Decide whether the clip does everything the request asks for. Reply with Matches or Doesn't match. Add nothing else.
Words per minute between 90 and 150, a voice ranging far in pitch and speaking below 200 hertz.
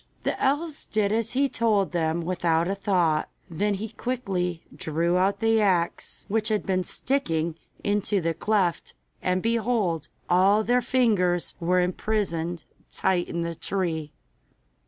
Doesn't match